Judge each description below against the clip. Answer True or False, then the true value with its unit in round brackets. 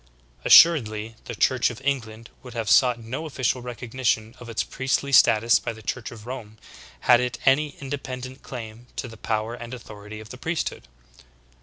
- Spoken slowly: False (175 wpm)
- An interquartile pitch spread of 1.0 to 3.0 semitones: True (2.7 semitones)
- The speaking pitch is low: True (120 Hz)